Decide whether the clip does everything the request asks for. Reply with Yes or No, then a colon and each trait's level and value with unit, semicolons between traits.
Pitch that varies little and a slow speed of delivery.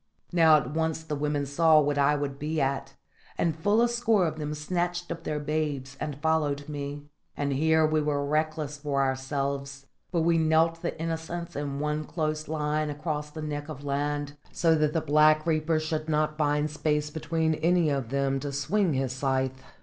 No: narrow, 1.8 semitones; average, 190 wpm